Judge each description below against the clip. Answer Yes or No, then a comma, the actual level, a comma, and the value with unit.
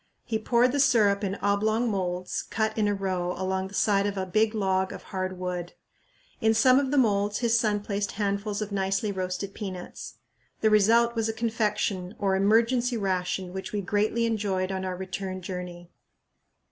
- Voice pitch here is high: Yes, high, 200 Hz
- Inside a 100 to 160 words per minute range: No, average, 180 wpm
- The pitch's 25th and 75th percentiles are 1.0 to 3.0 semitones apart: Yes, average, 2.7 semitones